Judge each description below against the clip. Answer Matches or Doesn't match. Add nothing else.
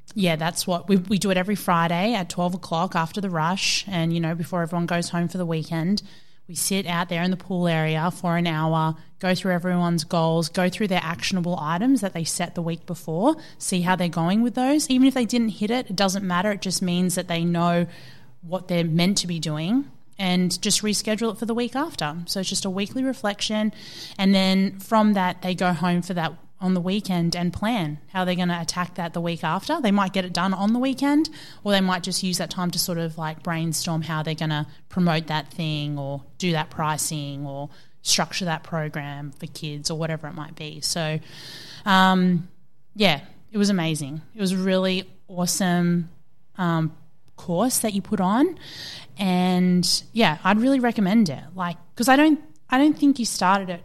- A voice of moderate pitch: Matches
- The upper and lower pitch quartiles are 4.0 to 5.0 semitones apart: Doesn't match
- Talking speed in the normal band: Doesn't match